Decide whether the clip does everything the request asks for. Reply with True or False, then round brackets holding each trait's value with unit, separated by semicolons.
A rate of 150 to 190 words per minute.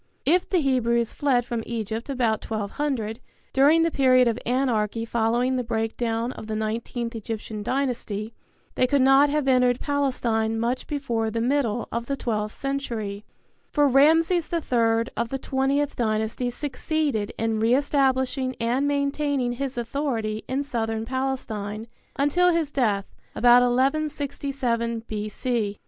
False (135 wpm)